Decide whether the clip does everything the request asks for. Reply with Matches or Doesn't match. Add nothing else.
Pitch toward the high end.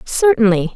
Matches